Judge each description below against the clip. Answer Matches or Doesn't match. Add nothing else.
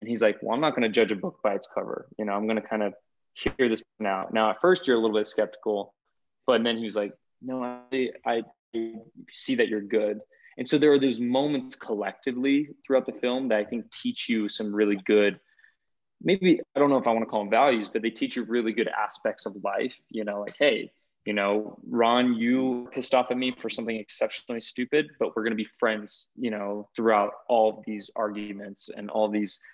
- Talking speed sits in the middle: Doesn't match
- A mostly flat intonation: Doesn't match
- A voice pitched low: Matches